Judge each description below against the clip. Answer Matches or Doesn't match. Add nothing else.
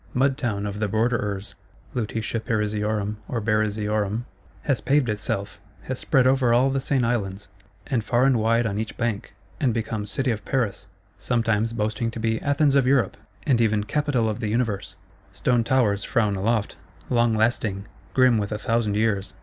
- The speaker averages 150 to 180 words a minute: Matches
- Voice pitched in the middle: Doesn't match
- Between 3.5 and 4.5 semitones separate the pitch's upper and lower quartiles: Doesn't match